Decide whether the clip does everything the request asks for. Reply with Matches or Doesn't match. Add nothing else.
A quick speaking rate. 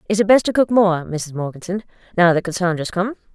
Matches